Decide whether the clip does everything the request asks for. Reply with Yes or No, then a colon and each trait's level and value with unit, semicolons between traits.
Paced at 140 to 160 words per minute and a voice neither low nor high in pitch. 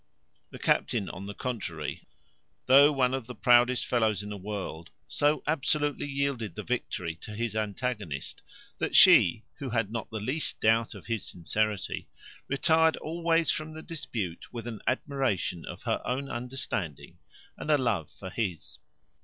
No: average, 155 wpm; low, 115 Hz